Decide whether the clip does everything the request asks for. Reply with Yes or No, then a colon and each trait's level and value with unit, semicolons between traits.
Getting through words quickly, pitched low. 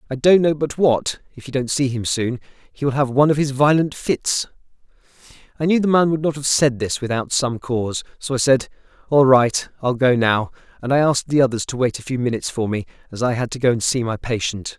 Yes: fast, 245 wpm; low, 130 Hz